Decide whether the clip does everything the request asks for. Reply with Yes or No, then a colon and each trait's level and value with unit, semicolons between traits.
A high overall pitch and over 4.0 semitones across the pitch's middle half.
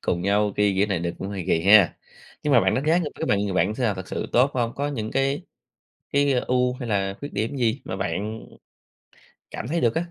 No: low, 110 Hz; average, 5.2 semitones